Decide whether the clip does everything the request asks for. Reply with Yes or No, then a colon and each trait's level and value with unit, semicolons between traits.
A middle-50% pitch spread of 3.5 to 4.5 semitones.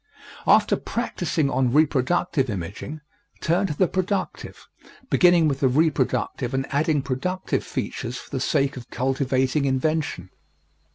Yes: average, 3.8 semitones